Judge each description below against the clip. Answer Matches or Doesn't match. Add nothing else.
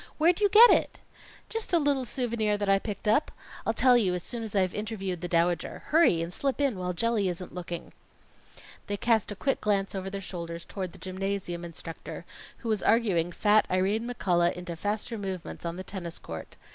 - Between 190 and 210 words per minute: Matches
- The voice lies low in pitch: Doesn't match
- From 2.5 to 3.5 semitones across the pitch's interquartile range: Doesn't match